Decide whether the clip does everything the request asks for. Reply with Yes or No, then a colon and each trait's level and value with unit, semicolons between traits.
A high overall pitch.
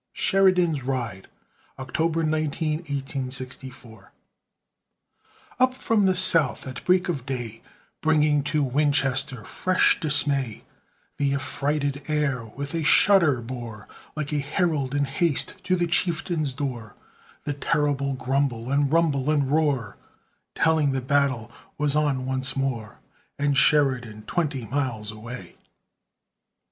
No: medium, 140 Hz